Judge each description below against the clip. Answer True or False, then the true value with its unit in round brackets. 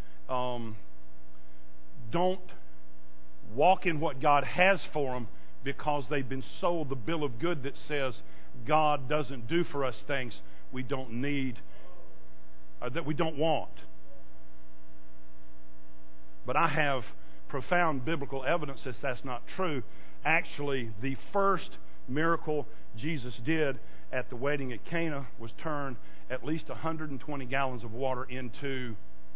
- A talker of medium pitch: False (130 Hz)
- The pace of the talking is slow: True (130 wpm)